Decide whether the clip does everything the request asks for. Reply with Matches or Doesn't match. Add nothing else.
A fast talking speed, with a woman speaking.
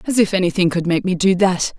Matches